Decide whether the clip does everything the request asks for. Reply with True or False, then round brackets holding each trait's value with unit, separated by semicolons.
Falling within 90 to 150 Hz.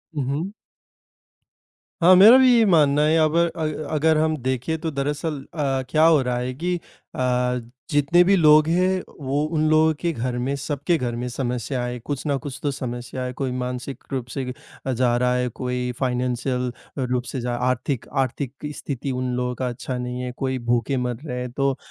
True (135 Hz)